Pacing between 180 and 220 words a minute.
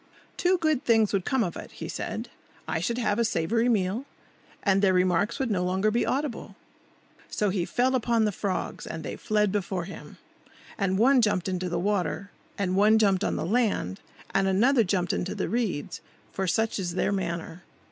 Yes: average, 190 wpm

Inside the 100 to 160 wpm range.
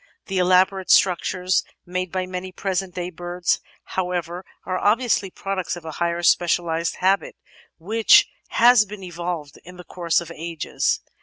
Yes: average, 150 wpm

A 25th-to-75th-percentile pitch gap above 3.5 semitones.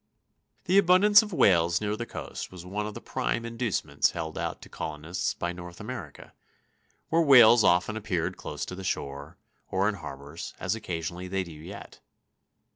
Yes: wide, 5.5 semitones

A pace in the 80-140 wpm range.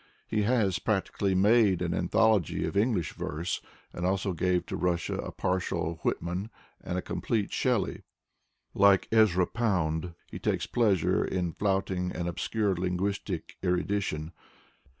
Yes: slow, 135 wpm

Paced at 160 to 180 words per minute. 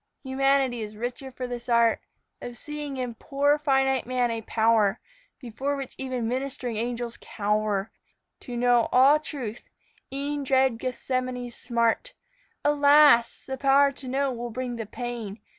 No: average, 140 wpm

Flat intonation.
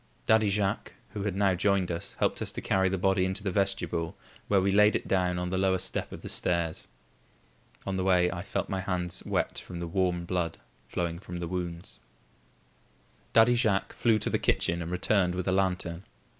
Yes: narrow, 1.9 semitones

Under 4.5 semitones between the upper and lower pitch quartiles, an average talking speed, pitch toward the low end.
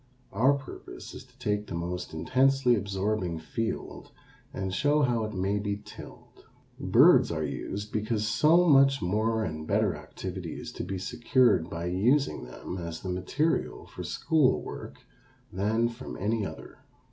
No: wide, 5.4 semitones; average, 155 wpm; low, 105 Hz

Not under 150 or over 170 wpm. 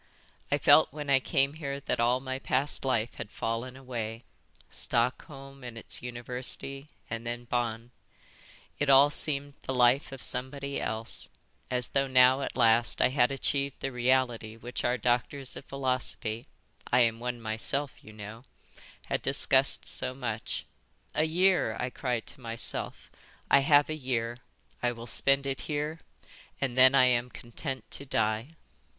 Yes: average, 155 wpm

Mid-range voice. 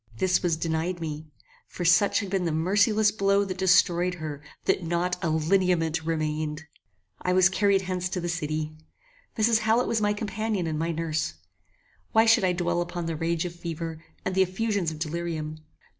Yes: medium, 175 Hz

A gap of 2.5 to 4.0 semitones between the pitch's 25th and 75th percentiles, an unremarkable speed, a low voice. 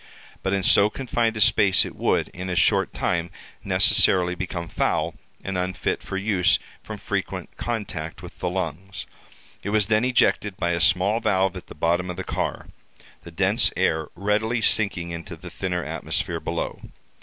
Yes: average, 3.0 semitones; average, 165 wpm; very low, 95 Hz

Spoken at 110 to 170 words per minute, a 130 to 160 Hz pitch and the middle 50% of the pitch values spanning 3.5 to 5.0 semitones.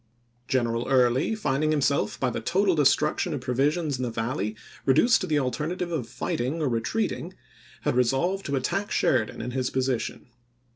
Yes: average, 165 wpm; low, 135 Hz; average, 4.3 semitones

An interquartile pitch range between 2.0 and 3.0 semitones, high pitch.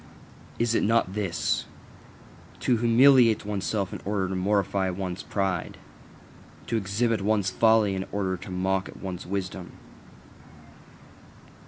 No: average, 2.7 semitones; low, 100 Hz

